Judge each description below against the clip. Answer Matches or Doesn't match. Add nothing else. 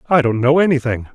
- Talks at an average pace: Doesn't match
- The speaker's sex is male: Matches